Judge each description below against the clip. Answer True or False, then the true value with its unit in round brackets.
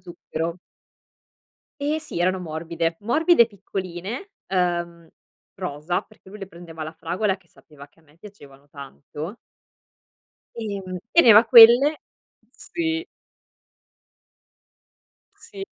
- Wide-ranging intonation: True (5.8 semitones)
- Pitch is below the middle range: False (185 Hz)